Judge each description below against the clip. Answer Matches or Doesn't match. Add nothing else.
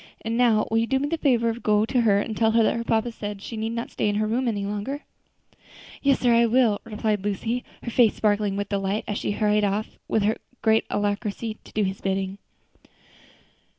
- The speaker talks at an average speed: Doesn't match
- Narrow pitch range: Matches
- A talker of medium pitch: Doesn't match